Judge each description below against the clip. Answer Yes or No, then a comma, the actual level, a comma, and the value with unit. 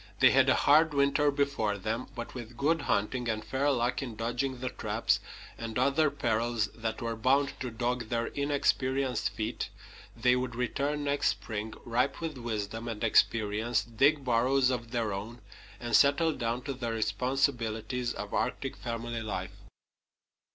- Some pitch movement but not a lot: Yes, average, 3.3 semitones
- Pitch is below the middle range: Yes, low, 120 Hz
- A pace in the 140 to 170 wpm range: Yes, average, 160 wpm